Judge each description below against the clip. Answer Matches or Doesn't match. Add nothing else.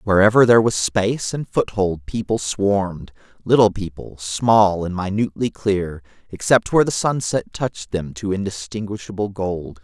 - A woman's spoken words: Doesn't match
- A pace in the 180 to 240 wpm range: Doesn't match